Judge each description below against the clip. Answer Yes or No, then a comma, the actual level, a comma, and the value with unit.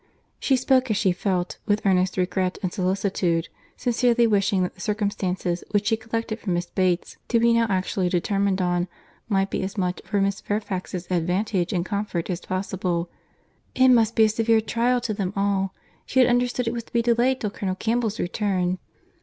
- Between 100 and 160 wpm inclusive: No, average, 185 wpm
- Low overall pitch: No, high, 200 Hz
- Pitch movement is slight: No, average, 3.6 semitones